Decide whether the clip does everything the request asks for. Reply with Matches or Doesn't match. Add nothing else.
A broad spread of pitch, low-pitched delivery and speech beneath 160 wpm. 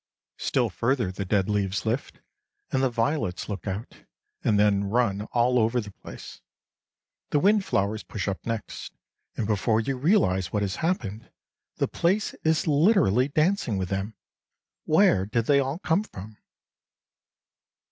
Matches